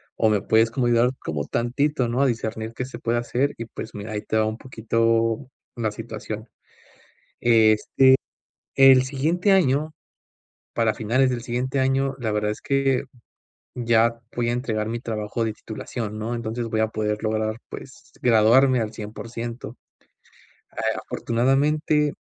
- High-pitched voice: No, low, 115 Hz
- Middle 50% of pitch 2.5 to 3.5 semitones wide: Yes, average, 2.9 semitones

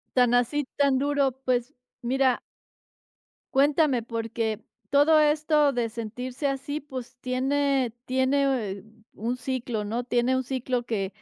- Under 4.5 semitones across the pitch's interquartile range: Yes, average, 2.8 semitones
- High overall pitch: Yes, very high, 255 Hz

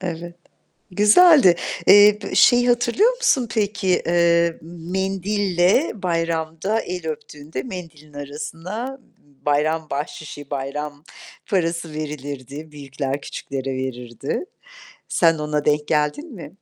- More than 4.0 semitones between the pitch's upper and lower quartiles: Yes, average, 4.7 semitones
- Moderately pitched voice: Yes, medium, 165 Hz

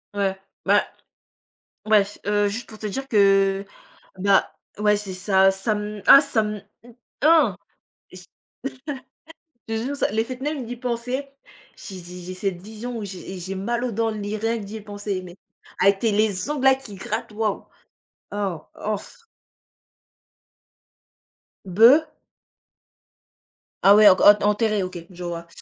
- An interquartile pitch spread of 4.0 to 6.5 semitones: No, average, 2.9 semitones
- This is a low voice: No, high, 210 Hz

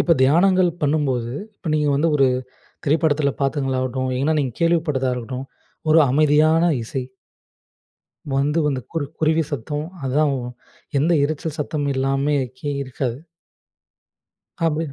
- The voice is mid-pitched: Yes, medium, 145 Hz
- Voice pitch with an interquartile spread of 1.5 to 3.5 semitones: Yes, average, 2.8 semitones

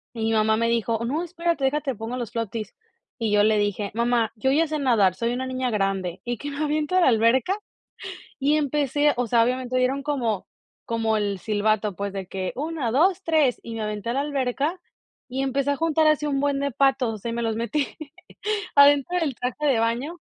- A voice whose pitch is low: No, very high, 250 Hz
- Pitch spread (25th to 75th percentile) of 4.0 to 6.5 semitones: Yes, average, 4.4 semitones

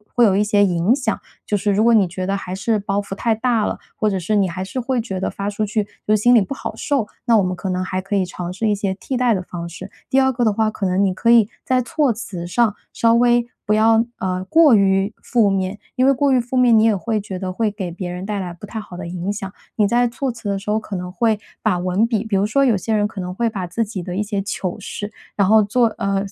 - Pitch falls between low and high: No, high, 205 Hz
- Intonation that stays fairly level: No, average, 3.4 semitones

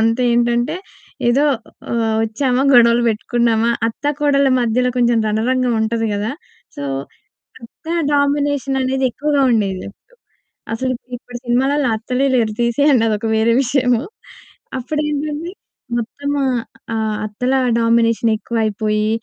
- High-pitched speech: Yes, high, 240 Hz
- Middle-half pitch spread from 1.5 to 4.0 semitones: Yes, average, 3.1 semitones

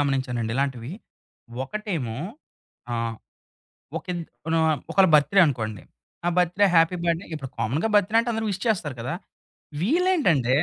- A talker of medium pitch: Yes, medium, 160 Hz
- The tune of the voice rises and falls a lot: Yes, wide, 7.2 semitones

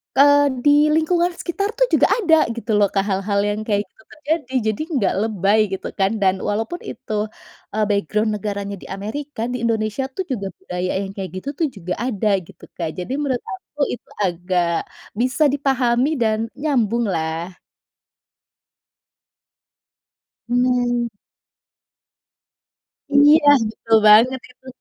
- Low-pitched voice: No, high, 225 Hz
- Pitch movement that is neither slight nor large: No, wide, 5.8 semitones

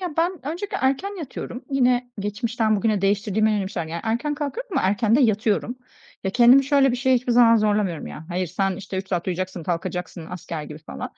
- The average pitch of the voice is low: No, high, 215 Hz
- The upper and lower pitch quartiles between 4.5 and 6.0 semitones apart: Yes, wide, 5.6 semitones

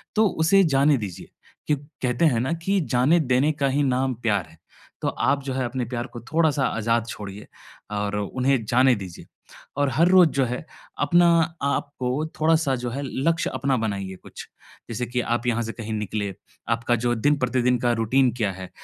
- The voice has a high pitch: No, low, 125 Hz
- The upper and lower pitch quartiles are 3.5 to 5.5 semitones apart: Yes, average, 3.9 semitones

